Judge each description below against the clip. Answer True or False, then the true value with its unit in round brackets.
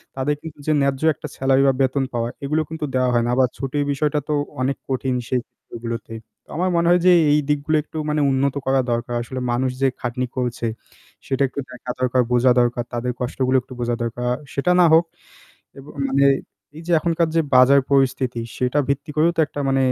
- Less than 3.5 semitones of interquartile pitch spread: True (2.8 semitones)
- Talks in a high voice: False (135 Hz)